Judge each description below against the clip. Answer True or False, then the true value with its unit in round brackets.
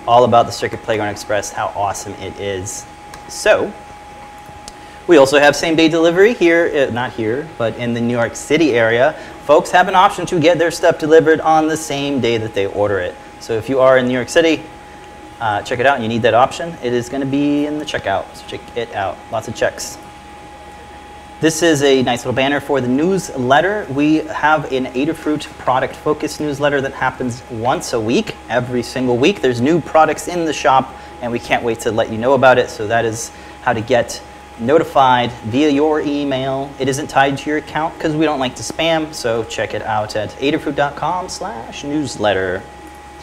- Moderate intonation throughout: True (4.6 semitones)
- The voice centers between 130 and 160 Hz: True (135 Hz)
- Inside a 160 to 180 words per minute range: False (195 wpm)